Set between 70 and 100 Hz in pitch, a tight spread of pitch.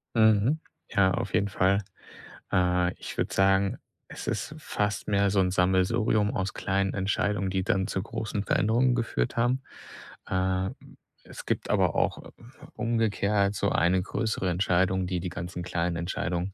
Yes: very low, 95 Hz; narrow, 2.2 semitones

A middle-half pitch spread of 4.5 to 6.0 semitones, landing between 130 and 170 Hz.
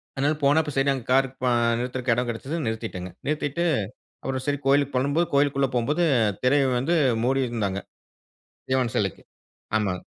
No: average, 3.1 semitones; low, 135 Hz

